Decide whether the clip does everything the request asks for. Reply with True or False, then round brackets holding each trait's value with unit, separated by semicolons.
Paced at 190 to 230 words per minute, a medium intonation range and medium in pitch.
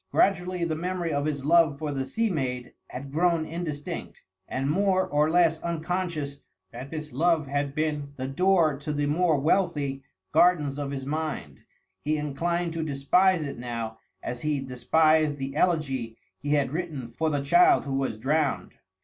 False (165 wpm; 3.5 semitones; 150 Hz)